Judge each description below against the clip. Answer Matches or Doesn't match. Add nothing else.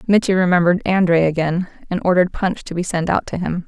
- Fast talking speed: Matches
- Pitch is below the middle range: Doesn't match